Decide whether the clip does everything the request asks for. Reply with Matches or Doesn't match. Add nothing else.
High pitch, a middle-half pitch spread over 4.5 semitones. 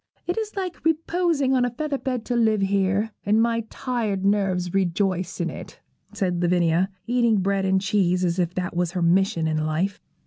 Matches